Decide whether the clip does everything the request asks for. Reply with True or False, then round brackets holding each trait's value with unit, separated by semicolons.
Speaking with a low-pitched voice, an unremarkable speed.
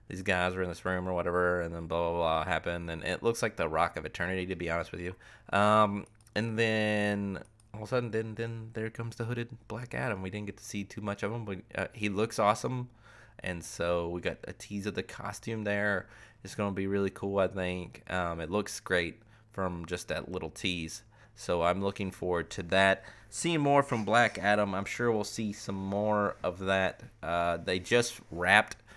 False (100 Hz; 215 wpm)